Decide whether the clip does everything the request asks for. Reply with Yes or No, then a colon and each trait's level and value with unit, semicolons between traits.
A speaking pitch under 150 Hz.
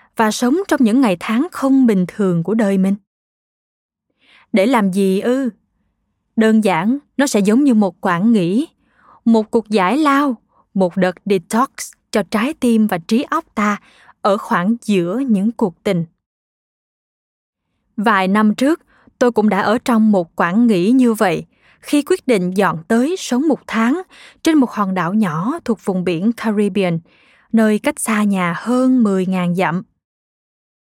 No: high, 220 Hz